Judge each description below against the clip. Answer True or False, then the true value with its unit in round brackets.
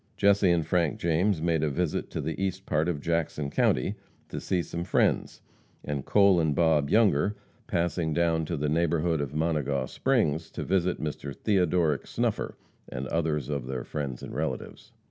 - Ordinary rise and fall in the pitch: True (3.0 semitones)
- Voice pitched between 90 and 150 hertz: False (80 Hz)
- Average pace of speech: True (170 wpm)